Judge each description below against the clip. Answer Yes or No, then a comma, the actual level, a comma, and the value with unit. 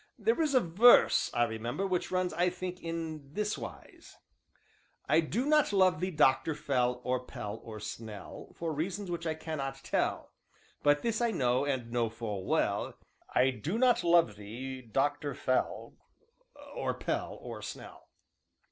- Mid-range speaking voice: Yes, medium, 155 Hz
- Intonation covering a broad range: Yes, wide, 6.6 semitones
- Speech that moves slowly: No, average, 155 wpm